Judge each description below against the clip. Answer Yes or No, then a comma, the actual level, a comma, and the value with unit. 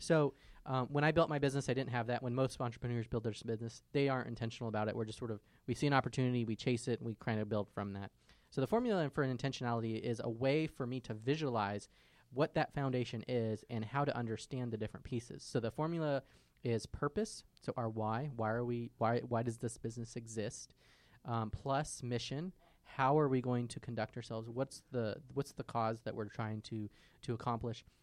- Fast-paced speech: Yes, fast, 220 wpm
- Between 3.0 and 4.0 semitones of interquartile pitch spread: Yes, average, 3.3 semitones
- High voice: No, low, 120 Hz